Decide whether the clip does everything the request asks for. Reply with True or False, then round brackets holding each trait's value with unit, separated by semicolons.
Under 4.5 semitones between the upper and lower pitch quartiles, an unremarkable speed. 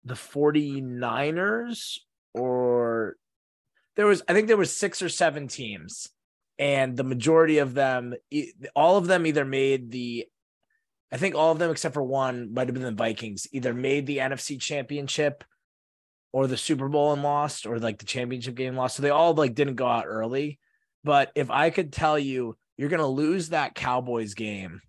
True (3.9 semitones; 180 wpm)